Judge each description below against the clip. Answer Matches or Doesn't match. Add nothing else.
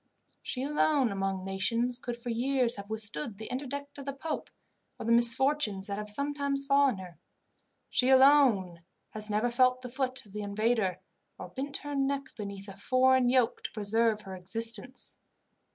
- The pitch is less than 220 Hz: Doesn't match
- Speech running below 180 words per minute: Matches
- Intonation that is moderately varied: Matches